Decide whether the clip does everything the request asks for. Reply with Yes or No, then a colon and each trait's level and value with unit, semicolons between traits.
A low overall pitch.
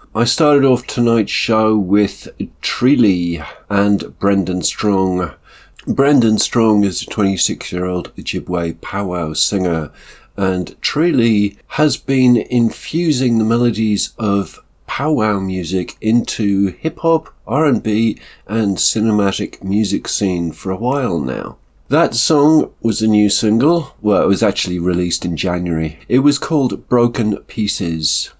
Yes: low, 105 Hz